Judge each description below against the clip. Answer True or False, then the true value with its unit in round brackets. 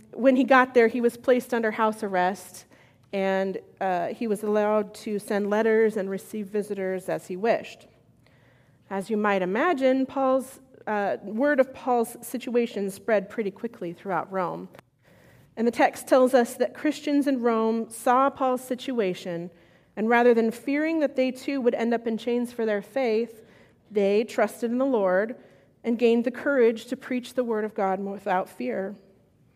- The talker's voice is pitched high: True (225 Hz)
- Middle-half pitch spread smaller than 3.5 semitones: False (4.2 semitones)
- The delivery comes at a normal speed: True (170 wpm)